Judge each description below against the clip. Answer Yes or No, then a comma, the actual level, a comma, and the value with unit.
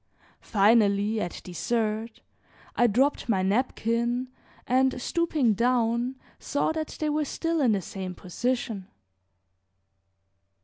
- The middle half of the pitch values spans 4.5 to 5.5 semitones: No, average, 3.8 semitones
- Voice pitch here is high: Yes, high, 235 Hz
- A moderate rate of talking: No, slow, 105 wpm